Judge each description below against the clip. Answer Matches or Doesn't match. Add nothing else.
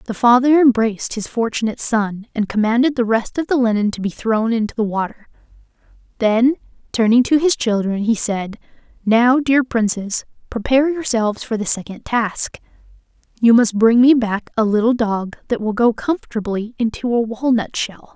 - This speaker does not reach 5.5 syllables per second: Matches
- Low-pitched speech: Doesn't match